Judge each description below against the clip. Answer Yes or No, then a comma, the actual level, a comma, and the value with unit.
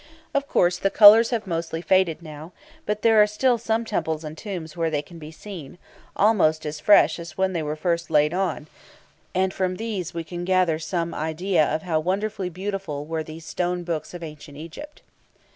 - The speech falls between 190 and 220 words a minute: Yes, average, 195 wpm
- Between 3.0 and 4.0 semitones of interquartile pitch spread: Yes, average, 3.7 semitones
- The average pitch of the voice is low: No, medium, 175 Hz